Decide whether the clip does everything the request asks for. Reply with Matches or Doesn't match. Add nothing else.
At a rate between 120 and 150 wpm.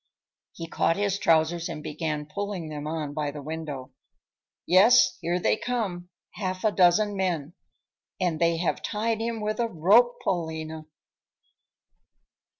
Matches